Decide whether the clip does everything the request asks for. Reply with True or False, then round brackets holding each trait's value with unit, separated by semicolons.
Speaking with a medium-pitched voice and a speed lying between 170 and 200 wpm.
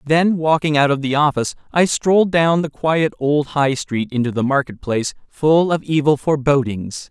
True (145 Hz; 185 wpm)